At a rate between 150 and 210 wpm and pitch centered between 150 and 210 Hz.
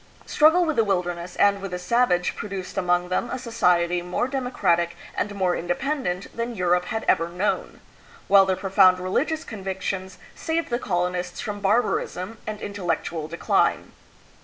Yes: average, 155 wpm; high, 190 Hz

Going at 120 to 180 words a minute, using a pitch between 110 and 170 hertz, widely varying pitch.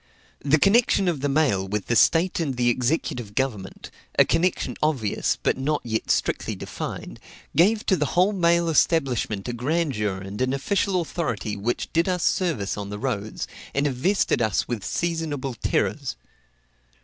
Yes: average, 160 wpm; medium, 140 Hz; wide, 7.3 semitones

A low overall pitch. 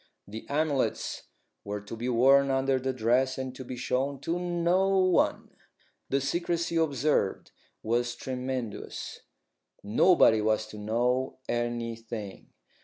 Yes: low, 130 Hz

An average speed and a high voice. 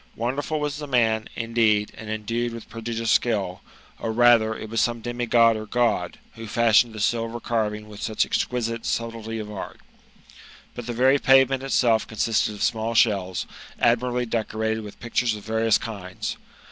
No: average, 170 wpm; low, 115 Hz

